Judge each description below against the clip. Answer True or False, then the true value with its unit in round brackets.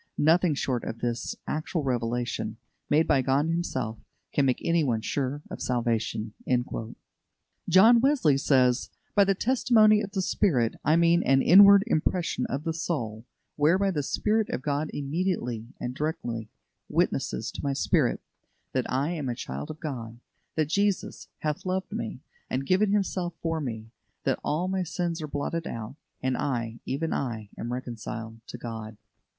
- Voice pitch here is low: False (145 Hz)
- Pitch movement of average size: False (6.3 semitones)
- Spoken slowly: False (155 wpm)